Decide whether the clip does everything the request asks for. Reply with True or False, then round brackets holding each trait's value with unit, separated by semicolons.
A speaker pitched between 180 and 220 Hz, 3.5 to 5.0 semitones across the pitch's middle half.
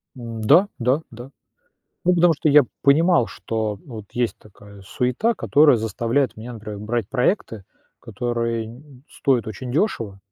False (120 Hz; 4.2 semitones)